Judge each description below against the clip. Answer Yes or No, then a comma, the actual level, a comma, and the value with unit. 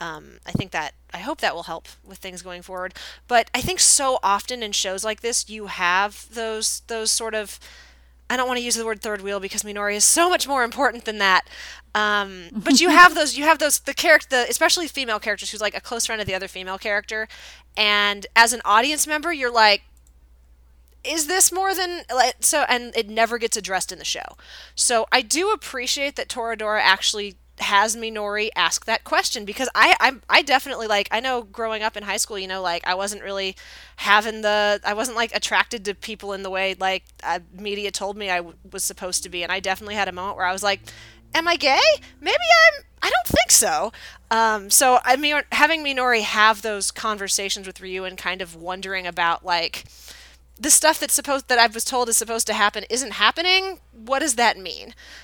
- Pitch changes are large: No, average, 4.3 semitones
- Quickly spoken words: Yes, fast, 215 wpm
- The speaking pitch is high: Yes, high, 215 Hz